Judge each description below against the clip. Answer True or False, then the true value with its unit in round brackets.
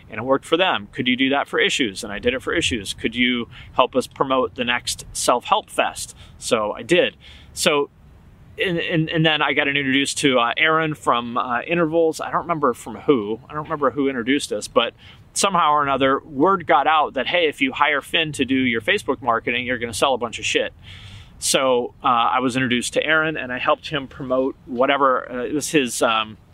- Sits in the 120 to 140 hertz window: True (135 Hz)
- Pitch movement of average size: True (4.0 semitones)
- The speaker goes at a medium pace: False (220 wpm)